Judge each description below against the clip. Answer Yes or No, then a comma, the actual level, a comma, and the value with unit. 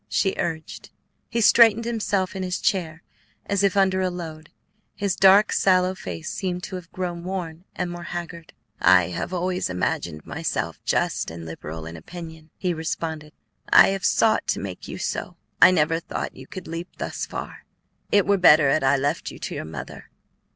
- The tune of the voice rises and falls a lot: No, average, 3.3 semitones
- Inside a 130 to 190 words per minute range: Yes, average, 180 wpm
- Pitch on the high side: No, medium, 175 Hz